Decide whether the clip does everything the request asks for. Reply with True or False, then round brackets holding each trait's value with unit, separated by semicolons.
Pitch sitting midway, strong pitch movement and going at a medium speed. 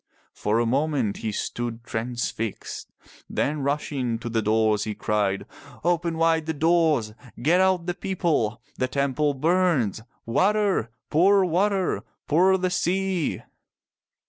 False (150 Hz; 7.3 semitones; 125 wpm)